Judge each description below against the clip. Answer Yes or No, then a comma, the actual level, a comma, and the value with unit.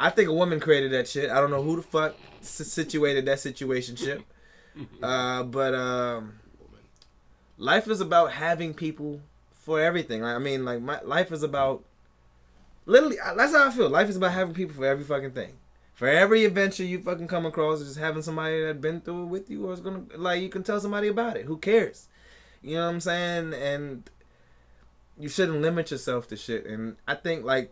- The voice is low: No, medium, 155 Hz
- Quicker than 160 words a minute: Yes, average, 200 wpm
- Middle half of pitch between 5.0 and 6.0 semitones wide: Yes, wide, 5.4 semitones